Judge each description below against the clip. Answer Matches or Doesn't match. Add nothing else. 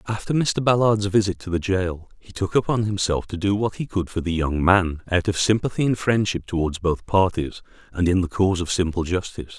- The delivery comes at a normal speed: Doesn't match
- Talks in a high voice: Doesn't match